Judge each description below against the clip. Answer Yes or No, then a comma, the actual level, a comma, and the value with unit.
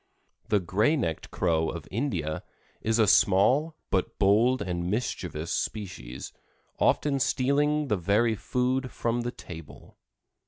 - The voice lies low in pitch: Yes, low, 105 Hz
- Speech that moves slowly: Yes, slow, 125 wpm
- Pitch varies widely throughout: Yes, wide, 6.4 semitones